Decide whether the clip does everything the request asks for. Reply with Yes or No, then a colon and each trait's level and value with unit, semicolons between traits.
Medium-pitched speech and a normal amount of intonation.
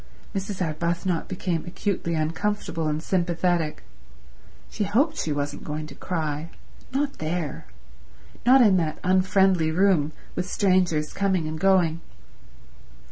Yes: medium, 175 Hz; average, 3.5 semitones